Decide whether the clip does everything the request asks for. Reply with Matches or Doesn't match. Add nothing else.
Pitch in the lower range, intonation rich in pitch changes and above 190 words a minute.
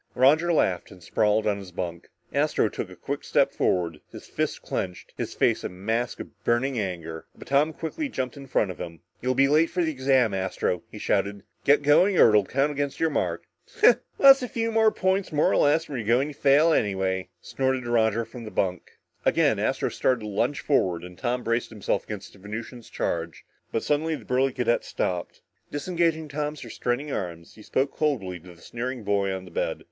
Matches